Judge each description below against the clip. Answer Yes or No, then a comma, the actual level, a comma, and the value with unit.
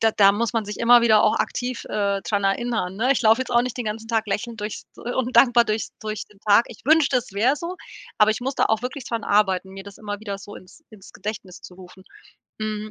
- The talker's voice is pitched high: Yes, high, 215 Hz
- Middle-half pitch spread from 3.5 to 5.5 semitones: No, average, 2.9 semitones